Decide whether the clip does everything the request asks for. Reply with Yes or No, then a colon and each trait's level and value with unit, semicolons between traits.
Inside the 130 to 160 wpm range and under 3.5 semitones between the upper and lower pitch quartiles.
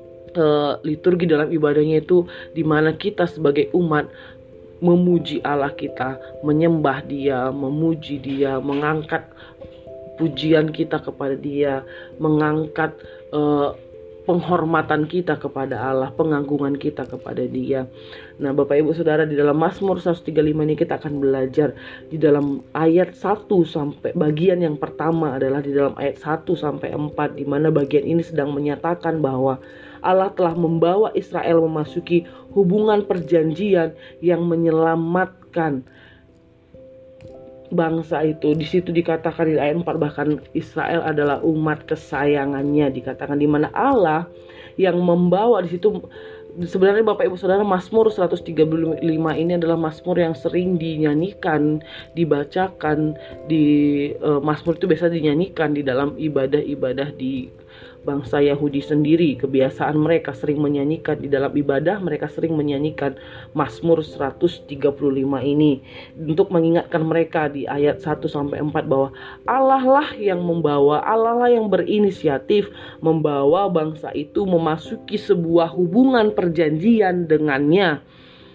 No: average, 120 wpm; average, 3.0 semitones